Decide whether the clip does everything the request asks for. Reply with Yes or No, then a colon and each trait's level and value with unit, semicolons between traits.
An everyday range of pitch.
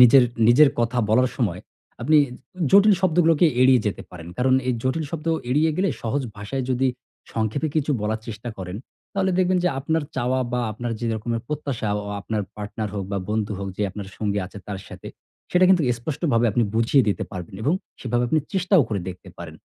No: wide, 6.3 semitones